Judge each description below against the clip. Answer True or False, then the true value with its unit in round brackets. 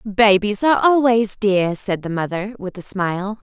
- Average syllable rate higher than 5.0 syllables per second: False (4.6 syllables/s)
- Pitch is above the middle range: True (205 Hz)